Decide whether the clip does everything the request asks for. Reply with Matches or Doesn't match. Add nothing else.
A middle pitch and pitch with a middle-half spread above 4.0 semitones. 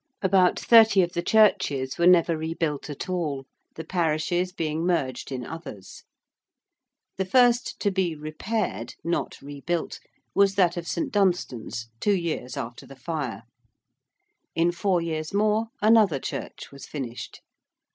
Matches